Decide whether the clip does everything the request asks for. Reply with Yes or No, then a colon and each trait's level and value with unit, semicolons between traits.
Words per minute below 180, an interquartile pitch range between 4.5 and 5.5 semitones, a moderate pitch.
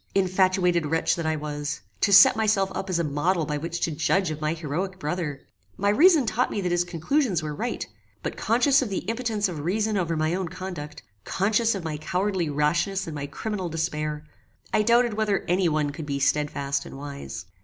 No: average, 200 wpm; average, 4.8 semitones; medium, 175 Hz